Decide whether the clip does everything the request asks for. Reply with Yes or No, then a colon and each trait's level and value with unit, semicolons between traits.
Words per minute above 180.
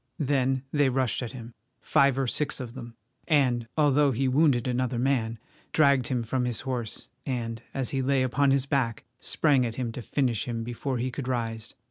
Yes: average, 190 wpm